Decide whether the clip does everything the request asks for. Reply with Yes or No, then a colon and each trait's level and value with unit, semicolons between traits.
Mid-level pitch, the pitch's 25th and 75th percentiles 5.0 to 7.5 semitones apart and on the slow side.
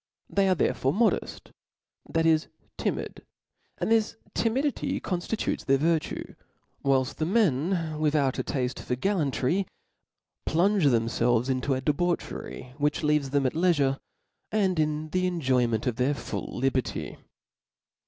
Yes: medium, 150 Hz; wide, 5.4 semitones; slow, 130 wpm